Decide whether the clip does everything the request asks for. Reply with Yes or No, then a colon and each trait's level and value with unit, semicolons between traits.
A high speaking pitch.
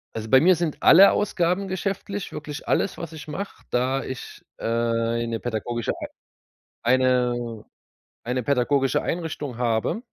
No: low, 130 Hz